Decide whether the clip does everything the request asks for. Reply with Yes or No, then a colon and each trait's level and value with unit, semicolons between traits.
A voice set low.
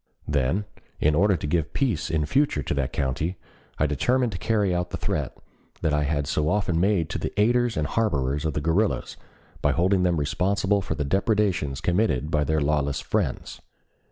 Yes: very low, 80 Hz